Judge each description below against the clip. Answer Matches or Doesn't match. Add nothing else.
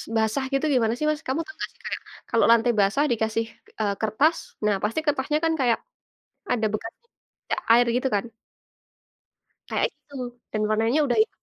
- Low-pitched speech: Doesn't match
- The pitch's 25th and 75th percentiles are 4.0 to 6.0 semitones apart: Matches